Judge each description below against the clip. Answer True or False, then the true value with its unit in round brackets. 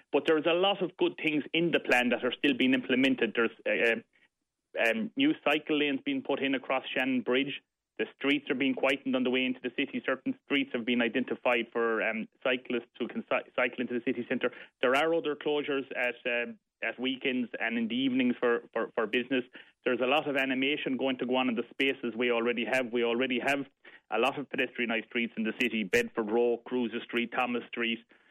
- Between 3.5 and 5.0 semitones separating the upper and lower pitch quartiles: False (2.7 semitones)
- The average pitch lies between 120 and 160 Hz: True (130 Hz)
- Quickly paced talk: True (215 wpm)